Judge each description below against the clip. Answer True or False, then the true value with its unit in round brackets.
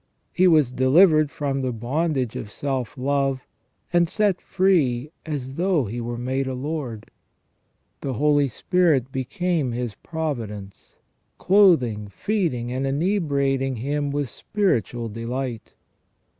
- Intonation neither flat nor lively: True (4.6 semitones)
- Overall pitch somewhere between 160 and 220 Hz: False (135 Hz)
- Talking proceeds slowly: True (120 wpm)